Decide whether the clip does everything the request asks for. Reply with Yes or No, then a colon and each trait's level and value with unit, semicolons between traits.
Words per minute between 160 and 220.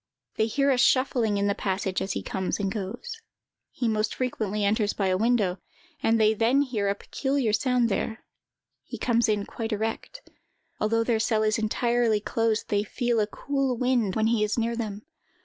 Yes: average, 185 wpm